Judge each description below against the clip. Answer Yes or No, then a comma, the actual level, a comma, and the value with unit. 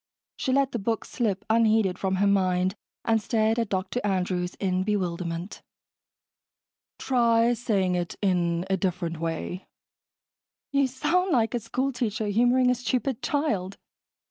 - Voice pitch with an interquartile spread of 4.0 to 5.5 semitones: Yes, average, 4.6 semitones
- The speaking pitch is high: Yes, high, 210 Hz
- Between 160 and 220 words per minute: No, average, 140 wpm